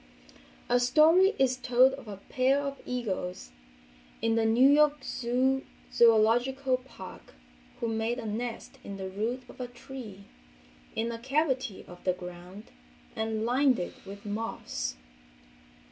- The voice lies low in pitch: No, high, 240 Hz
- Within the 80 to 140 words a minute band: Yes, slow, 135 wpm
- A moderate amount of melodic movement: Yes, average, 3.6 semitones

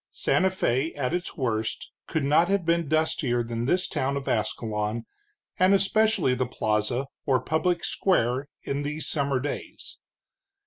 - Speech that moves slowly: No, average, 145 wpm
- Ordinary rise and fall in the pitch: No, wide, 5.9 semitones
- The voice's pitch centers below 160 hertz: Yes, medium, 140 Hz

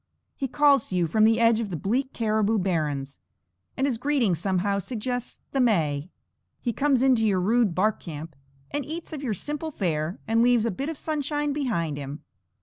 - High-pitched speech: Yes, high, 225 Hz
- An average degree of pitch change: No, wide, 6.9 semitones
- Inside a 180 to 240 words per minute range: Yes, average, 190 wpm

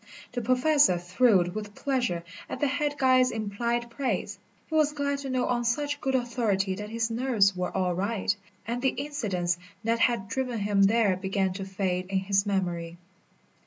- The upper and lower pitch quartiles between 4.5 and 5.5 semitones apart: Yes, average, 4.9 semitones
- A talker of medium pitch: No, high, 225 Hz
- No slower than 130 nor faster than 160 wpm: No, average, 175 wpm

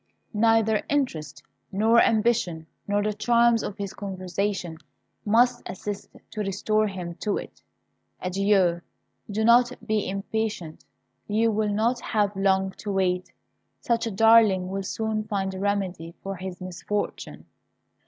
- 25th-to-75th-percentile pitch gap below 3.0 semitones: Yes, narrow, 2.6 semitones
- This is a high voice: Yes, high, 205 Hz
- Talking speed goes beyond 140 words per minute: No, slow, 135 wpm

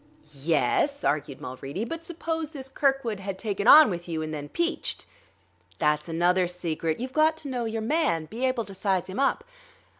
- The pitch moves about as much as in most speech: No, wide, 8.8 semitones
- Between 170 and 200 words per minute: Yes, average, 180 wpm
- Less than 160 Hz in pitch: No, high, 200 Hz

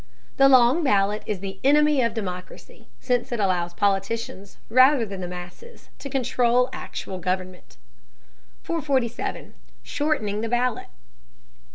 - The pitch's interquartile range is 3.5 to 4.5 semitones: No, average, 5.2 semitones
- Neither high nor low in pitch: No, high, 230 Hz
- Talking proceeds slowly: Yes, slow, 125 wpm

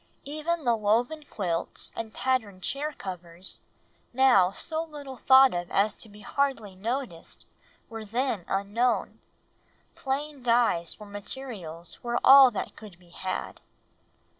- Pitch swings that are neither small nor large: No, wide, 5.7 semitones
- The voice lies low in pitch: No, high, 230 Hz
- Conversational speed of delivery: No, slow, 130 wpm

